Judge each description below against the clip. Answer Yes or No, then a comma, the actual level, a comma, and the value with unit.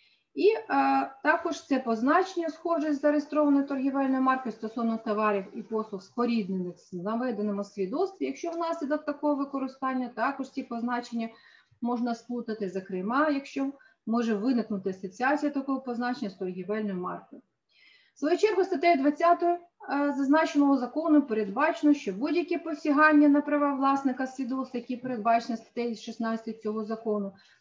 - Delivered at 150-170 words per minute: No, average, 130 wpm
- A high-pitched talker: Yes, very high, 265 Hz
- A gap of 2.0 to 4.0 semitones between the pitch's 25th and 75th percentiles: No, average, 4.8 semitones